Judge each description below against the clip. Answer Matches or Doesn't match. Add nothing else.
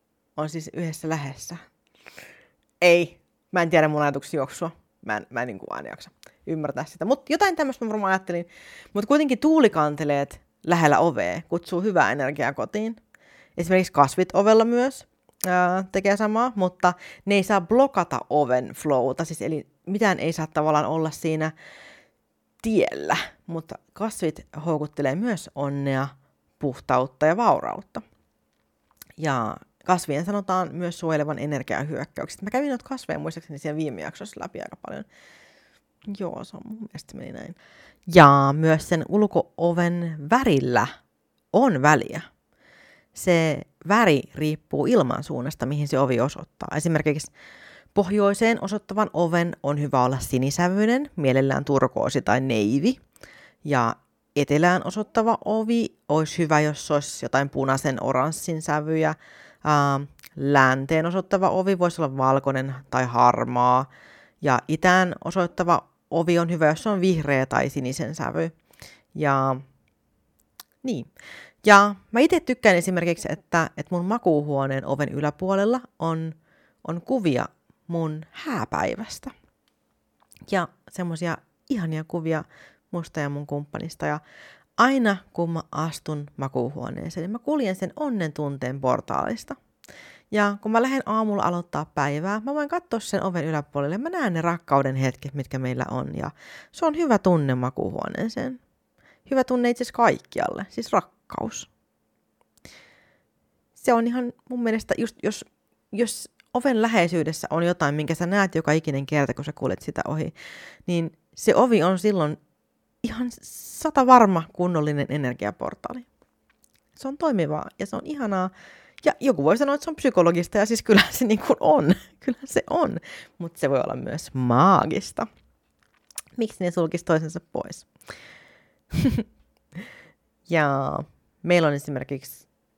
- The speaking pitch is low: Doesn't match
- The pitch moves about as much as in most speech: Doesn't match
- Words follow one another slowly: Doesn't match